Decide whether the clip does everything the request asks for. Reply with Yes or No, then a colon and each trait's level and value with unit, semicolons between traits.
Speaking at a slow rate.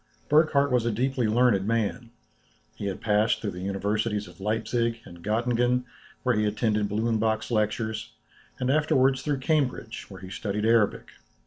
No: average, 150 wpm